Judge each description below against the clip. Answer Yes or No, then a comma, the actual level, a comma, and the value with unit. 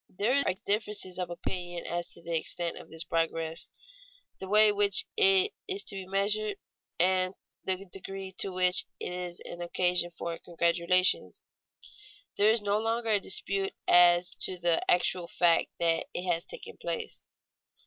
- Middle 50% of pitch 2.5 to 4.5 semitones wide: Yes, average, 2.8 semitones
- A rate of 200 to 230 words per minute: No, average, 165 wpm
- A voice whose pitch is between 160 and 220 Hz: Yes, medium, 185 Hz